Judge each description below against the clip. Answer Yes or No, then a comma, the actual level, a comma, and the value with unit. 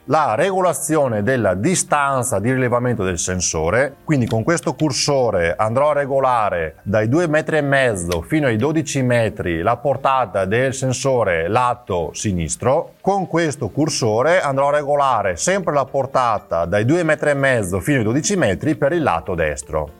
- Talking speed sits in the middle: Yes, average, 145 wpm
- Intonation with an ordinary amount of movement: No, wide, 5.9 semitones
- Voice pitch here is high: No, low, 135 Hz